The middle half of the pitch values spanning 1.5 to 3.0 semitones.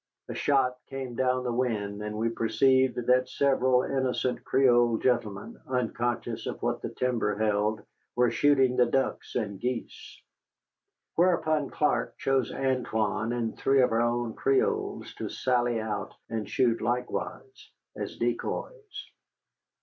Yes: narrow, 2.6 semitones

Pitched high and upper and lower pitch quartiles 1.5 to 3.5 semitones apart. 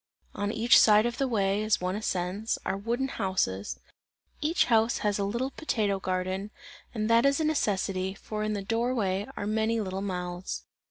Yes: high, 210 Hz; average, 3.1 semitones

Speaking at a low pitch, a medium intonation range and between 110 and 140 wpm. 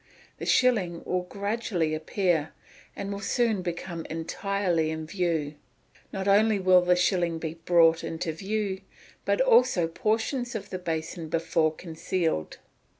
No: medium, 180 Hz; average, 3.5 semitones; slow, 135 wpm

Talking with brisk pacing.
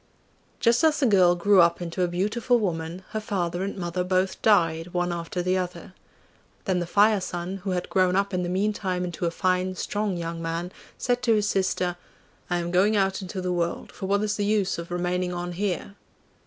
Yes: fast, 210 wpm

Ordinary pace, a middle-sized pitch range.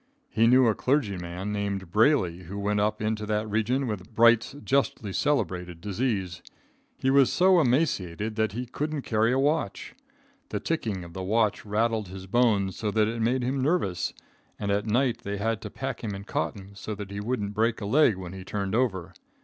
Yes: average, 190 wpm; average, 3.8 semitones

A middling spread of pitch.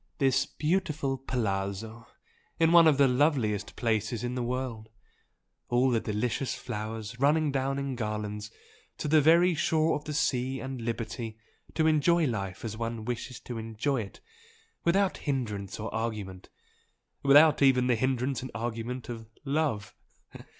Yes: average, 4.2 semitones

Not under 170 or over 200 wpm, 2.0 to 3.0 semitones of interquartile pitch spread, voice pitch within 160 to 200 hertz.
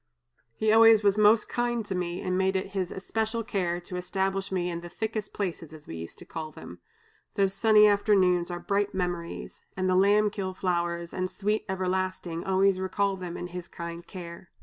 Yes: average, 195 wpm; average, 2.7 semitones; high, 190 Hz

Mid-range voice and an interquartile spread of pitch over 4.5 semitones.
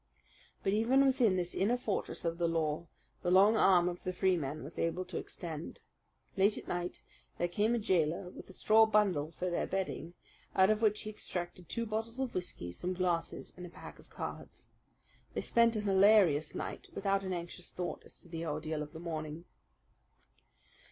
No: medium, 180 Hz; average, 3.9 semitones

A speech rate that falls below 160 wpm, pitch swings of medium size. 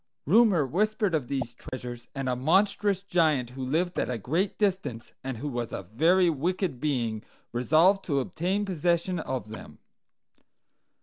No: average, 150 wpm; wide, 6.6 semitones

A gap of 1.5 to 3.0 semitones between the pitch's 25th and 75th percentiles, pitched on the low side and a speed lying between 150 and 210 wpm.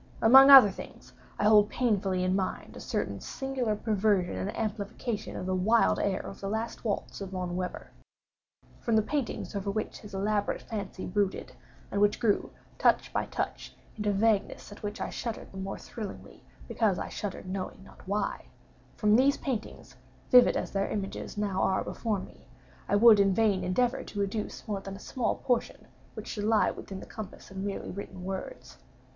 No: narrow, 2.5 semitones; high, 205 Hz; average, 180 wpm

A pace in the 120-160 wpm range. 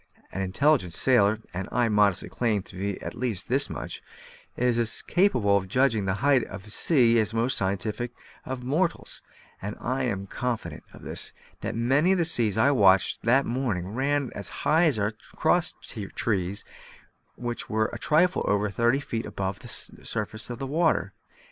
No: average, 180 wpm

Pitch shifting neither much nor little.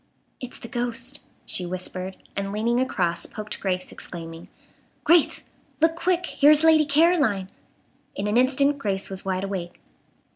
No: wide, 7.3 semitones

